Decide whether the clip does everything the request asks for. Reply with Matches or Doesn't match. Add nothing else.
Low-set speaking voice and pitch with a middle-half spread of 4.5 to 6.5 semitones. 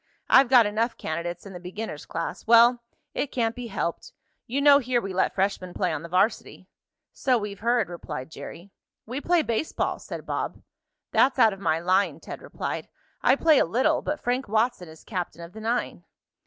Doesn't match